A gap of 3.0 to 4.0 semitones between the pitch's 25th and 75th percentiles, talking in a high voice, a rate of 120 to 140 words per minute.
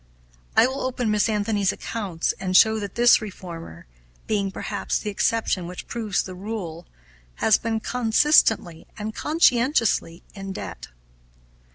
Yes: average, 3.7 semitones; high, 210 Hz; slow, 135 wpm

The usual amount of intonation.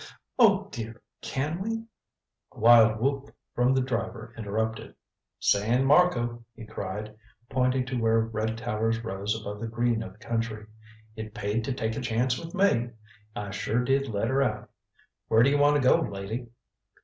Yes: average, 3.0 semitones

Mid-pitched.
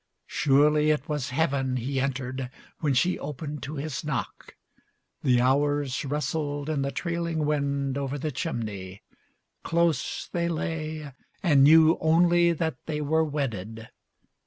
Yes: medium, 145 Hz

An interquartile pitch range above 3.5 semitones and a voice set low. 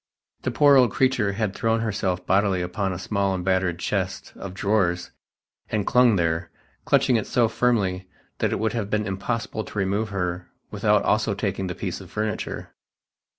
No: average, 2.9 semitones; low, 100 Hz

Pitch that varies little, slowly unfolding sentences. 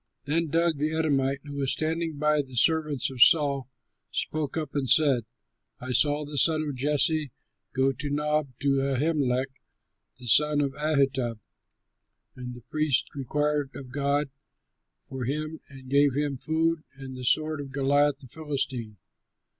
No: narrow, 2.3 semitones; average, 155 wpm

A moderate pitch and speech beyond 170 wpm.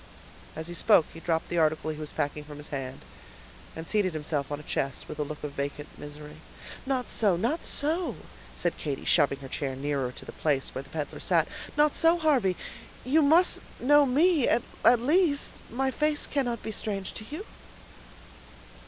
Yes: medium, 175 Hz; average, 185 wpm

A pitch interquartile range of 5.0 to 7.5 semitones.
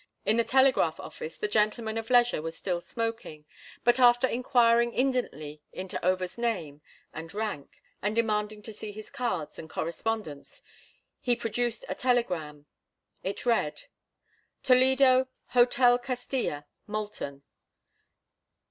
Yes: wide, 5.6 semitones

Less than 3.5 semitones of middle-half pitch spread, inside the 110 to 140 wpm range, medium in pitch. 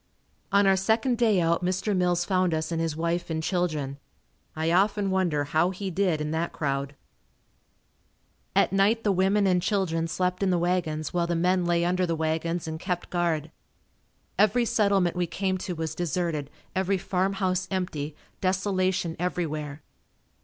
No: average, 2.8 semitones; average, 165 wpm; medium, 180 Hz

